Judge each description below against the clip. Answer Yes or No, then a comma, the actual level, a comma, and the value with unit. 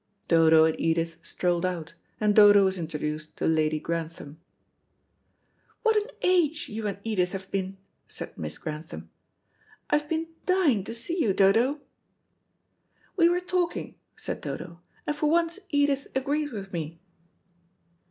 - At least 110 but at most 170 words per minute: Yes, average, 140 wpm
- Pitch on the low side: No, high, 200 Hz